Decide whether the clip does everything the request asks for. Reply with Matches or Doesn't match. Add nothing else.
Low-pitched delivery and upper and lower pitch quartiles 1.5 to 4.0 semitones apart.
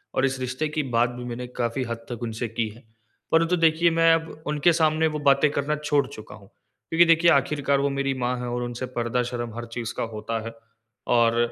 Doesn't match